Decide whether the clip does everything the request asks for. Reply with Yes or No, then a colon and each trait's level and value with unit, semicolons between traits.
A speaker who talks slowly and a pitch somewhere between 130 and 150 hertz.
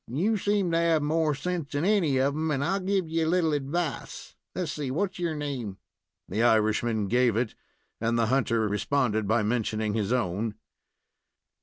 No: average, 175 wpm; medium, 140 Hz